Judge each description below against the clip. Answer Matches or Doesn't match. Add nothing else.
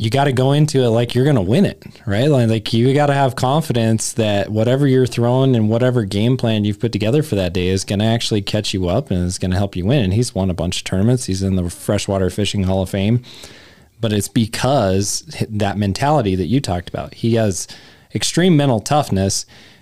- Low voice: Matches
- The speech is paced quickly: Matches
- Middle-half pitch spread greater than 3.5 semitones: Matches